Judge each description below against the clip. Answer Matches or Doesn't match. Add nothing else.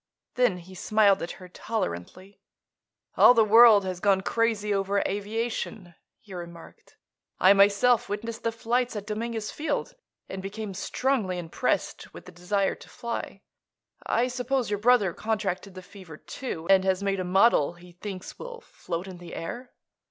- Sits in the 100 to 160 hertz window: Doesn't match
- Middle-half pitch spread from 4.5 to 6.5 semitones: Doesn't match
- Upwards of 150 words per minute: Matches